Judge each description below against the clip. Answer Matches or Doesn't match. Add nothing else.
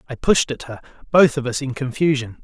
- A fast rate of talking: Matches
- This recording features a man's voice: Matches